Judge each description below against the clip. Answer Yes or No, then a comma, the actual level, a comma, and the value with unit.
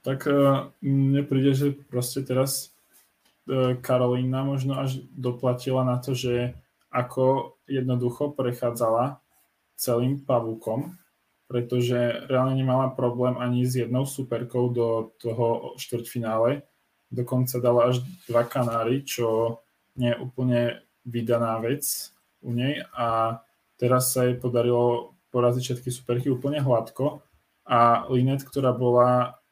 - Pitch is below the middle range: Yes, low, 125 Hz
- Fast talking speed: No, slow, 115 wpm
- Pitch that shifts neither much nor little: No, narrow, 1.8 semitones